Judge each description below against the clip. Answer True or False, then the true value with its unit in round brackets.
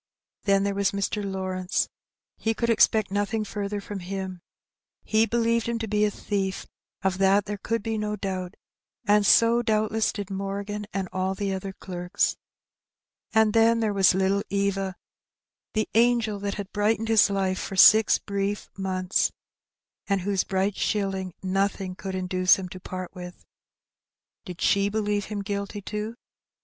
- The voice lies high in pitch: True (200 Hz)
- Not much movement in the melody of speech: True (1.9 semitones)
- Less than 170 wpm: True (160 wpm)